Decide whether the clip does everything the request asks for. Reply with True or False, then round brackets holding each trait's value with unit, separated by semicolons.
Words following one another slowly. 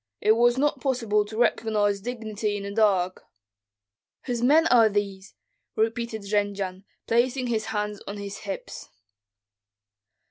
True (130 wpm)